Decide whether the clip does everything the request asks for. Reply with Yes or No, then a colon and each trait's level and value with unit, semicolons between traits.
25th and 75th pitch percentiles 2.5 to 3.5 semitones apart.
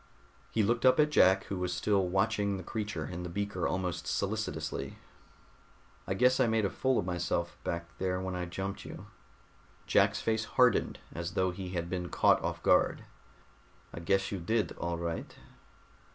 Yes: average, 2.8 semitones